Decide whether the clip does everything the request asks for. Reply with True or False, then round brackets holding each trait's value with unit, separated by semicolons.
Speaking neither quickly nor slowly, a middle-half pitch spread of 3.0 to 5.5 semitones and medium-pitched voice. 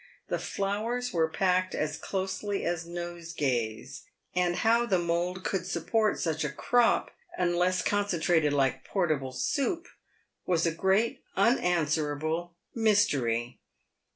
False (120 wpm; 4.1 semitones; 175 Hz)